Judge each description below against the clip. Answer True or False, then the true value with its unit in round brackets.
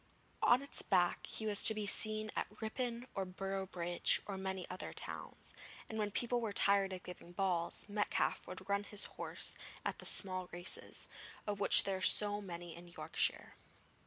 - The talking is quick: False (175 wpm)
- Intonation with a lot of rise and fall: False (2.5 semitones)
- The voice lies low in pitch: False (195 Hz)